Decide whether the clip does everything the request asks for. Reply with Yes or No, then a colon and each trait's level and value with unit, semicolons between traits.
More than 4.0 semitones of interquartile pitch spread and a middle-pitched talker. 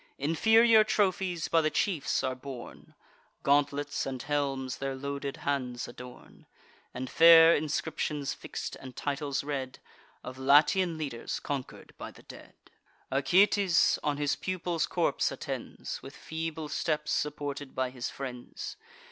No: average, 3.4 semitones; medium, 145 Hz